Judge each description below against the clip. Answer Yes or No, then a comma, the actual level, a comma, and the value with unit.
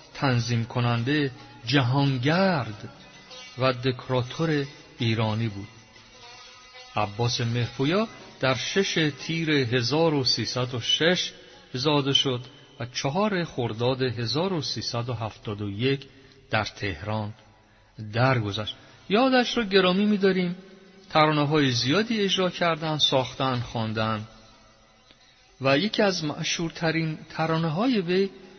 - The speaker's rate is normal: No, slow, 85 wpm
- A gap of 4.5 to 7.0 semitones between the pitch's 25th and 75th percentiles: Yes, wide, 5.6 semitones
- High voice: No, low, 135 Hz